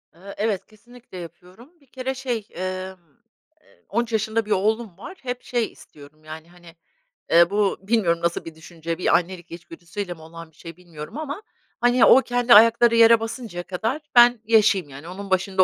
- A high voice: Yes, high, 200 Hz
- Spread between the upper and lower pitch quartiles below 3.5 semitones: No, average, 5.3 semitones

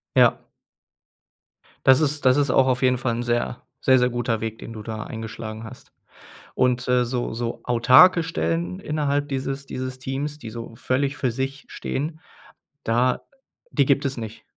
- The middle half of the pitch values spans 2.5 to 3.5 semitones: Yes, average, 2.9 semitones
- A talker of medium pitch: No, low, 130 Hz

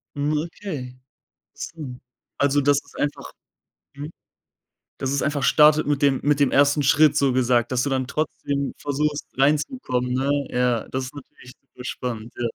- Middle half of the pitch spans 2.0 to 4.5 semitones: Yes, narrow, 2.5 semitones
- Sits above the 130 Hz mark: Yes, medium, 140 Hz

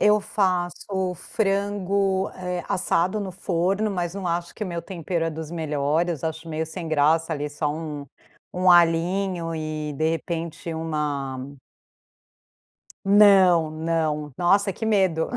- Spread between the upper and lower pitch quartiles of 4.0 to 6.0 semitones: No, average, 3.1 semitones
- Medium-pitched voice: Yes, medium, 170 Hz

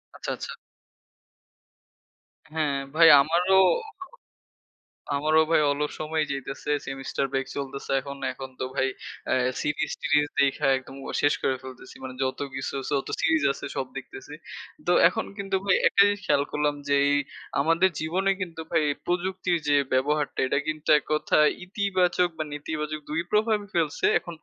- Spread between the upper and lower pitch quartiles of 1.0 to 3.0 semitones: No, average, 3.7 semitones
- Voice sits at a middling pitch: Yes, medium, 155 Hz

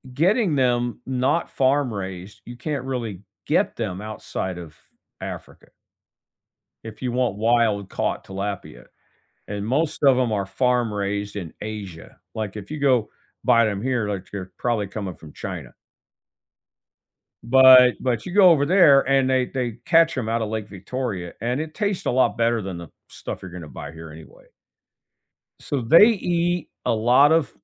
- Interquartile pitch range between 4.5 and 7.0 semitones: Yes, average, 4.8 semitones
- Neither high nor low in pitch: No, low, 115 Hz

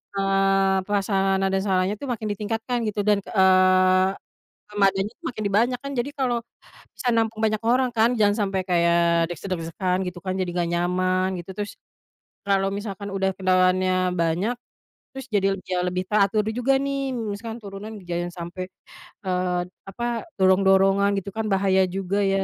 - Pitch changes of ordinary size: No, narrow, 2.3 semitones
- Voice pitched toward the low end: No, high, 195 Hz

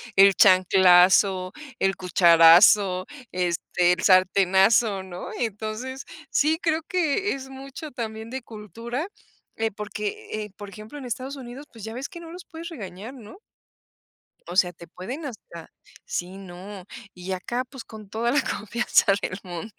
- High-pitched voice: Yes, high, 210 Hz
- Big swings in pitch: Yes, wide, 5.7 semitones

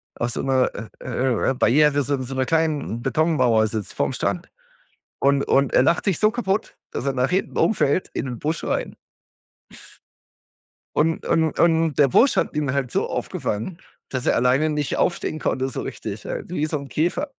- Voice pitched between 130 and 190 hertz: Yes, medium, 140 Hz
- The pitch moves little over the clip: No, average, 4.1 semitones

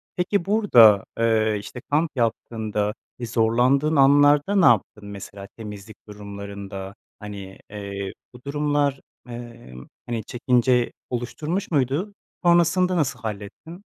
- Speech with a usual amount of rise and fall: No, wide, 5.9 semitones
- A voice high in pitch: No, low, 120 Hz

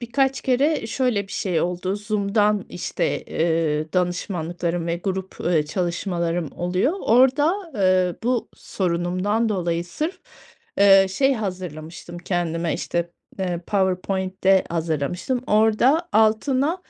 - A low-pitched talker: No, high, 190 Hz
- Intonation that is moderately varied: Yes, average, 4.3 semitones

